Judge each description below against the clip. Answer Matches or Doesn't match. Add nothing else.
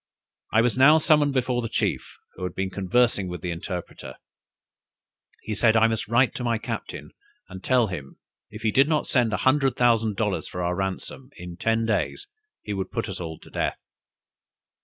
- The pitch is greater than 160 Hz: Doesn't match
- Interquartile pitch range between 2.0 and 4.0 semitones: Doesn't match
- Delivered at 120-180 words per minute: Doesn't match